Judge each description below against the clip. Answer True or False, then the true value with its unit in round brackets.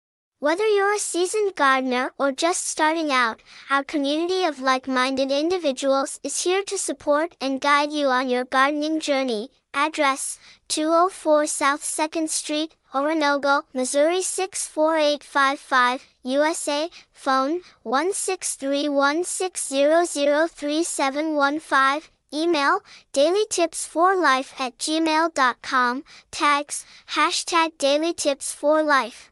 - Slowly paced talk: True (95 wpm)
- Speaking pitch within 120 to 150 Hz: False (295 Hz)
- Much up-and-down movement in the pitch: False (3.1 semitones)